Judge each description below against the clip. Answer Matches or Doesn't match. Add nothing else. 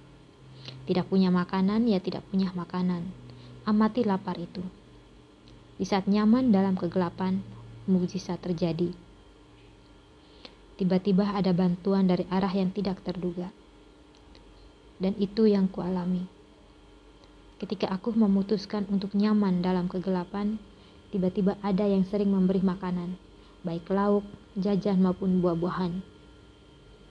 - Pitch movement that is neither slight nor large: Doesn't match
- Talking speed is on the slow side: Doesn't match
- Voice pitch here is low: Doesn't match